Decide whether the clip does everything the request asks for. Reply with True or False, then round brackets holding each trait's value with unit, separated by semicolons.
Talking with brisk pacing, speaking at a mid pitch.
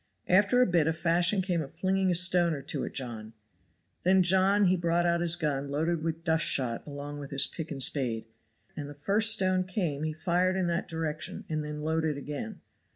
True (220 wpm; 165 Hz)